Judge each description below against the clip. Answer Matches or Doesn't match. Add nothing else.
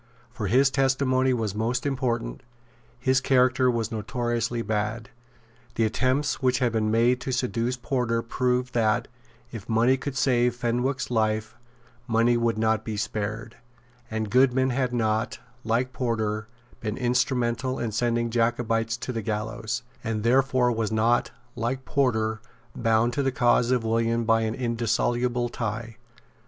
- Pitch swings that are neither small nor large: Doesn't match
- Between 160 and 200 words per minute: Doesn't match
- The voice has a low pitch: Matches